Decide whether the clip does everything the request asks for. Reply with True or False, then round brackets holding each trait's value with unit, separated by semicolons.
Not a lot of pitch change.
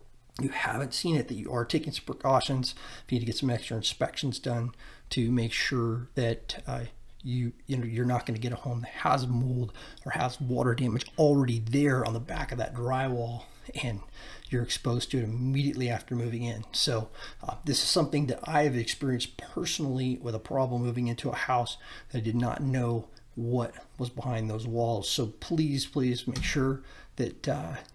True (2.1 semitones)